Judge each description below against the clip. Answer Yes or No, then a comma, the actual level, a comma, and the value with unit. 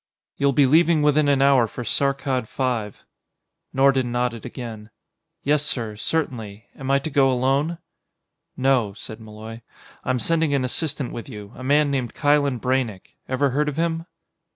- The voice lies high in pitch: No, low, 135 Hz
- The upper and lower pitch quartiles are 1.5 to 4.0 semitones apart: Yes, average, 3.3 semitones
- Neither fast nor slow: Yes, average, 155 wpm